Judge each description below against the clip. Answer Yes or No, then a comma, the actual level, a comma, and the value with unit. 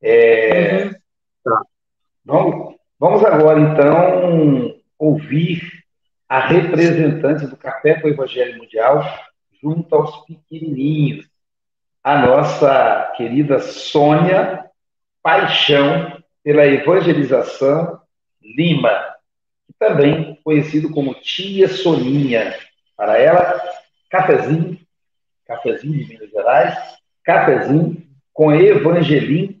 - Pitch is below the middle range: No, medium, 155 Hz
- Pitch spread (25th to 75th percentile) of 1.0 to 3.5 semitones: Yes, average, 3.1 semitones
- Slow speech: Yes, slow, 80 wpm